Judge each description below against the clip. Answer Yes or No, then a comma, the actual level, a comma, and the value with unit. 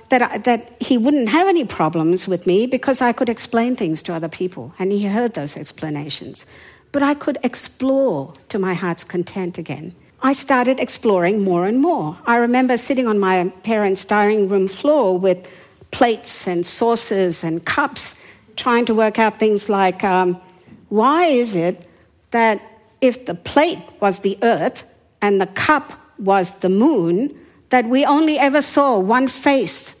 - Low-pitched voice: No, high, 220 Hz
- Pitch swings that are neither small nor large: No, wide, 5.8 semitones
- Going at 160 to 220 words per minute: Yes, average, 165 wpm